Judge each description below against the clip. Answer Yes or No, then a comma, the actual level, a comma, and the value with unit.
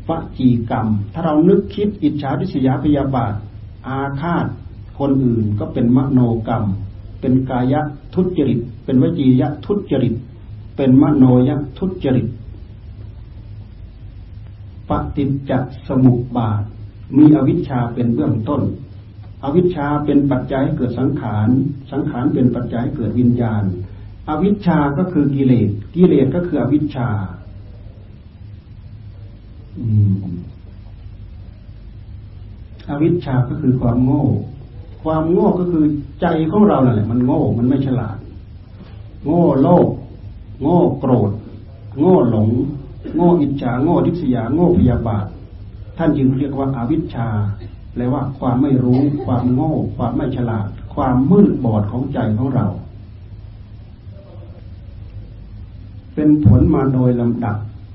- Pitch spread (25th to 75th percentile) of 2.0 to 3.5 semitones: No, average, 5.1 semitones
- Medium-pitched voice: No, low, 120 Hz